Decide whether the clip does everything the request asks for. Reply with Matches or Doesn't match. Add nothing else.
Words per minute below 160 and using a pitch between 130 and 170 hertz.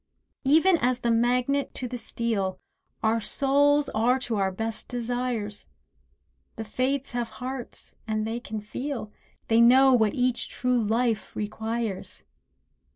Doesn't match